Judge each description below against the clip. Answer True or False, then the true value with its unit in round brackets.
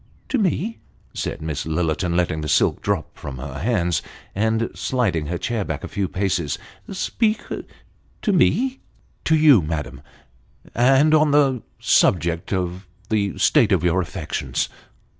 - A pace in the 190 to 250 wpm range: False (160 wpm)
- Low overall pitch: True (95 Hz)